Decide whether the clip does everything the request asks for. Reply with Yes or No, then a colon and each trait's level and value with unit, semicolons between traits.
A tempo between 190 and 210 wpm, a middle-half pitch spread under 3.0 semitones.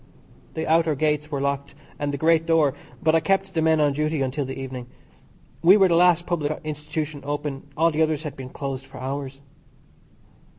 Yes: average, 195 wpm; narrow, 2.5 semitones